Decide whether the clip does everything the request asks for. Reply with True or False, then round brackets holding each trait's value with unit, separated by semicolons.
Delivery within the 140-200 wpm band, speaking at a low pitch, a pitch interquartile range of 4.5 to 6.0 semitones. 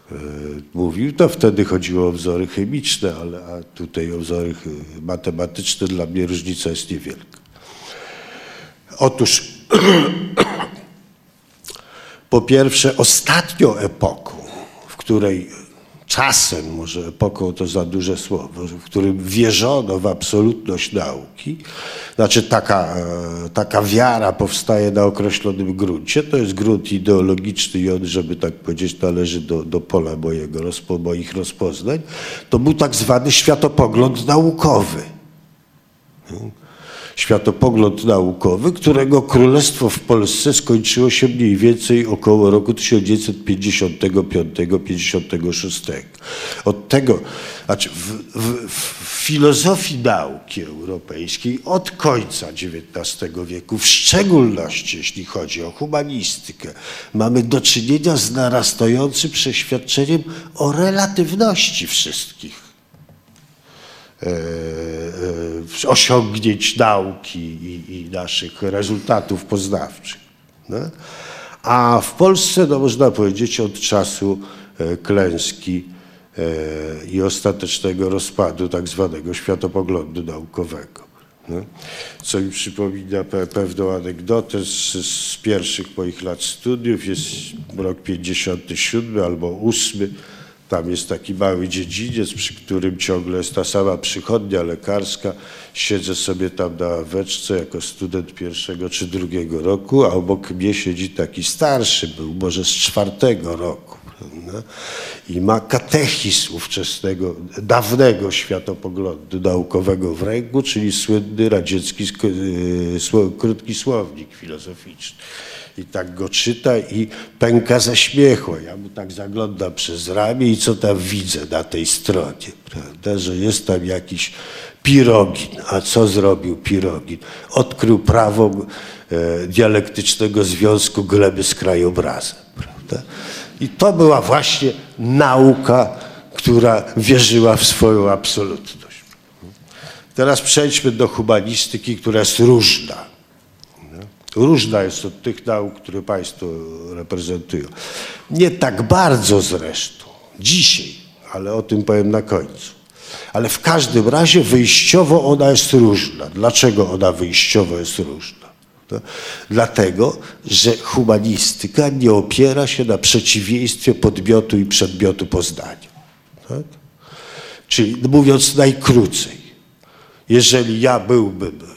False (110 wpm; 100 Hz; 4.9 semitones)